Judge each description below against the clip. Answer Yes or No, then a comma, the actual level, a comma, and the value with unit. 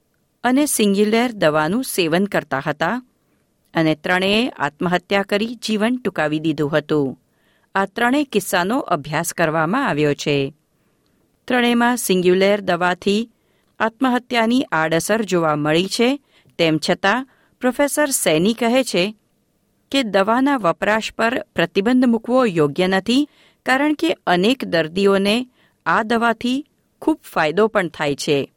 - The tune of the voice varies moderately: No, wide, 6.5 semitones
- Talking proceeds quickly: No, average, 115 wpm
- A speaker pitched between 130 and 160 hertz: No, high, 205 Hz